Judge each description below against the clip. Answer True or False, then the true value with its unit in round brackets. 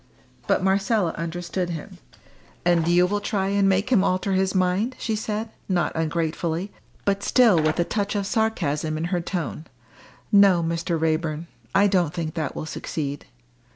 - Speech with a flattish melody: False (3.4 semitones)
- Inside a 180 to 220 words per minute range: False (160 wpm)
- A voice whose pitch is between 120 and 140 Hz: False (180 Hz)